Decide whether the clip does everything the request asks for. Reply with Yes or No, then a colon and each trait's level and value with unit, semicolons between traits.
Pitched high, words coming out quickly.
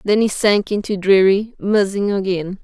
No: high, 200 Hz; average, 160 wpm